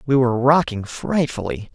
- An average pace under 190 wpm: Yes, average, 140 wpm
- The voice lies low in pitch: Yes, low, 130 Hz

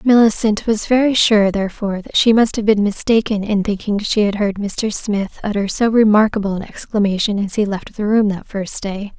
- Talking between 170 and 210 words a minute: Yes, average, 200 wpm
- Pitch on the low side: No, high, 210 Hz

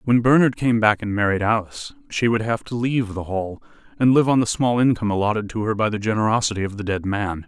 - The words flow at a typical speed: No, fast, 240 wpm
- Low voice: Yes, low, 110 Hz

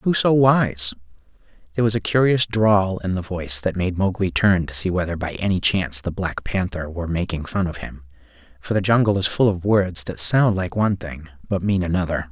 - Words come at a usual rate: No, fast, 215 wpm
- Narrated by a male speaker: Yes, male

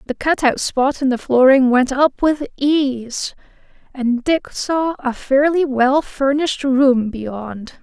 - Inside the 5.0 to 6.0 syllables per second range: No, 3.5 syllables/s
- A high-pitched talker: Yes, very high, 270 Hz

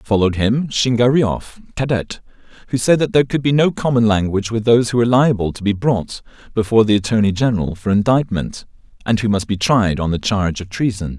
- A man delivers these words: Yes, male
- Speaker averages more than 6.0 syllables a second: Yes, 6.2 syllables/s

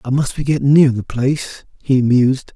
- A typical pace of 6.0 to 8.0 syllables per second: No, 5.2 syllables/s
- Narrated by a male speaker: Yes, male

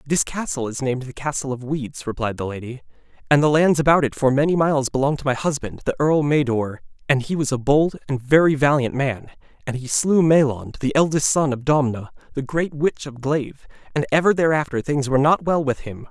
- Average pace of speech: No, fast, 215 wpm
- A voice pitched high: No, medium, 140 Hz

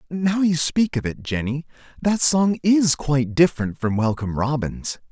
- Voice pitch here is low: No, medium, 150 Hz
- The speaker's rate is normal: Yes, average, 165 wpm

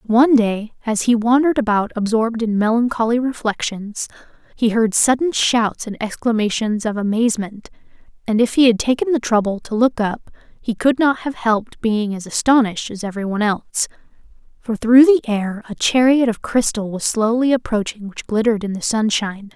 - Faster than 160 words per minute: Yes, average, 170 wpm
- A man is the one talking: No, female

